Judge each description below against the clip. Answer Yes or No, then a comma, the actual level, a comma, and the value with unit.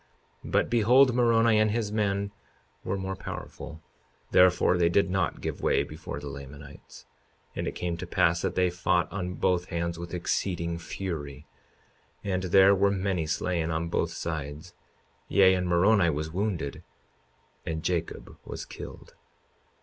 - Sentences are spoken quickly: No, average, 150 wpm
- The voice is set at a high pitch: No, very low, 90 Hz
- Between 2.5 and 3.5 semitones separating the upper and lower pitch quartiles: Yes, average, 2.9 semitones